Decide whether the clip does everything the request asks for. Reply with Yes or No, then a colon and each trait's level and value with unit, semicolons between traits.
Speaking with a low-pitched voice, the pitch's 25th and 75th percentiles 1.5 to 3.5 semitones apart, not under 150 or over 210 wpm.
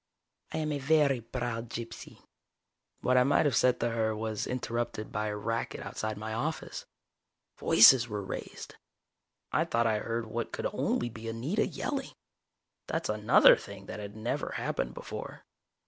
Yes: low, 115 Hz; average, 2.7 semitones; average, 160 wpm